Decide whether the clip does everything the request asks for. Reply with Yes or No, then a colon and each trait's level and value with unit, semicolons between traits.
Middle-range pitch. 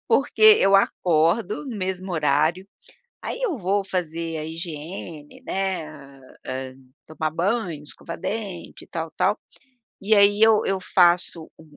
Yes: medium, 175 Hz